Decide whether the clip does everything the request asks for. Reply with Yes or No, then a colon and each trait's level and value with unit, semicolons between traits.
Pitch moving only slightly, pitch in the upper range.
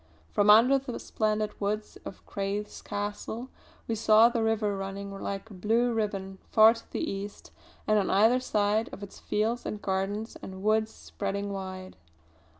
Yes: narrow, 2.0 semitones; high, 210 Hz